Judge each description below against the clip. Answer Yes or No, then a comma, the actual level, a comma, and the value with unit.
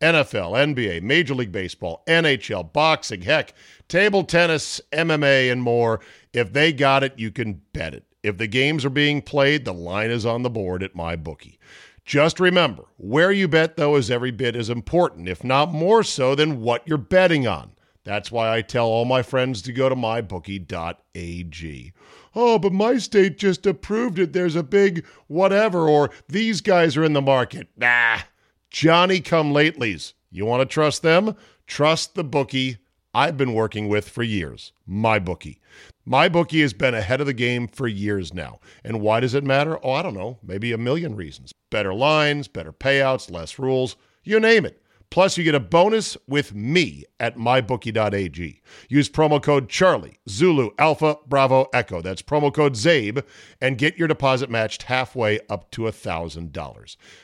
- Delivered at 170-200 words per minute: Yes, average, 175 wpm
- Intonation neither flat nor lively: No, wide, 6.0 semitones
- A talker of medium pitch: No, low, 130 Hz